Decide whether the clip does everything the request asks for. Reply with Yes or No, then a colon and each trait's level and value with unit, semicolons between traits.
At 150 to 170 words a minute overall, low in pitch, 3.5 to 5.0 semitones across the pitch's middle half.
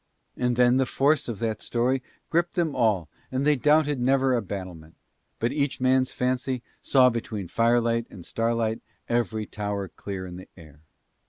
Yes: average, 165 wpm; low, 120 Hz; average, 3.9 semitones